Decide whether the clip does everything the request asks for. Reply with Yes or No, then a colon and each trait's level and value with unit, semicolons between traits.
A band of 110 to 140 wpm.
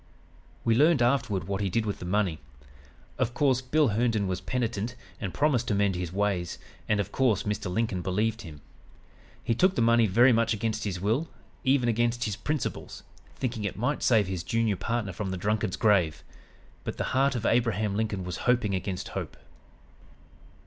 No: average, 180 wpm